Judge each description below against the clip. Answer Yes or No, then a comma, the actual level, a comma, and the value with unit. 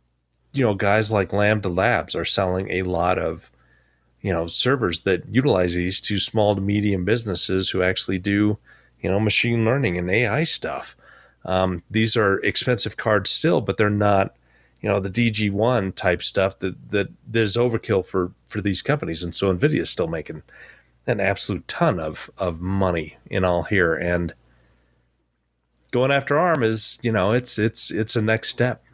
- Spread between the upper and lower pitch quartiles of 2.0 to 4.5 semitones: Yes, average, 3.7 semitones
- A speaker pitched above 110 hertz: No, very low, 95 Hz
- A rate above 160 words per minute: Yes, average, 170 wpm